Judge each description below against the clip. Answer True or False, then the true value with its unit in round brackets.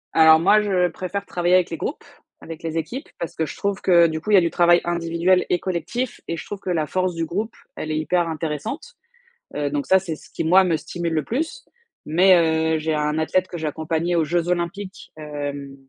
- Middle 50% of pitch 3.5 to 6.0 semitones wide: False (2.8 semitones)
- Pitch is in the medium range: True (170 Hz)